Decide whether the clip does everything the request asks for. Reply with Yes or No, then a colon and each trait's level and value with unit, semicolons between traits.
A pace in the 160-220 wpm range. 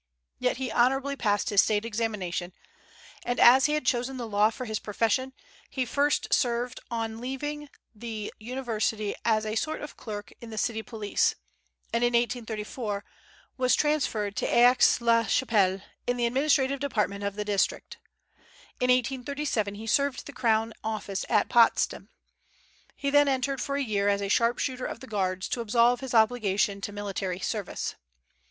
Yes: average, 165 wpm